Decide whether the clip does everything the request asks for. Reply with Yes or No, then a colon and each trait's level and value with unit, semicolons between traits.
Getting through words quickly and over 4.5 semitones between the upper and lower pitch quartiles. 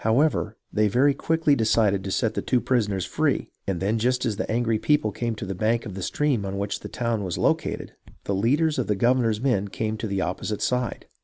No: fast, 225 wpm; average, 3.8 semitones